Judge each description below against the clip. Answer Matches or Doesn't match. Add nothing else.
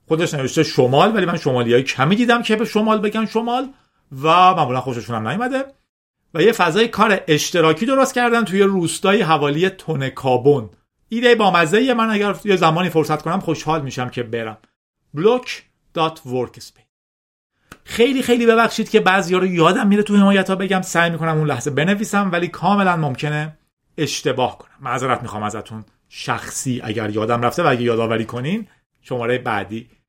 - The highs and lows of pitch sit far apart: Matches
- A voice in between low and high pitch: Matches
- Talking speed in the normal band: Doesn't match